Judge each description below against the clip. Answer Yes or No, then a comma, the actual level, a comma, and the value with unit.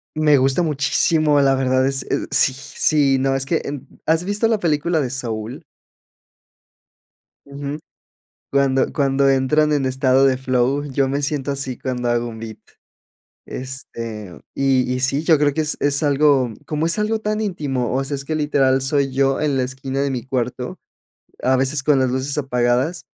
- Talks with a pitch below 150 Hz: Yes, low, 135 Hz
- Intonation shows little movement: Yes, narrow, 2.2 semitones